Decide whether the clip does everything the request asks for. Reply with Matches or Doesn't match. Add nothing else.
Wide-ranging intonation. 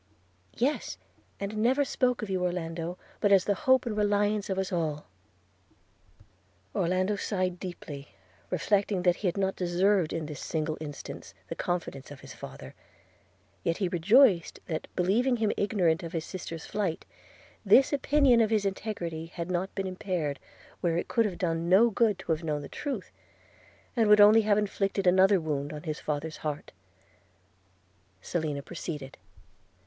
Doesn't match